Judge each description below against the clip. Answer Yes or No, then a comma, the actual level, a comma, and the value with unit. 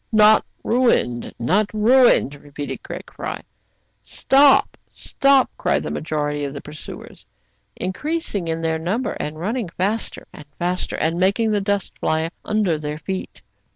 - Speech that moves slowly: No, average, 150 wpm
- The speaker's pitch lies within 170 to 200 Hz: Yes, medium, 185 Hz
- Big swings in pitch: Yes, wide, 5.9 semitones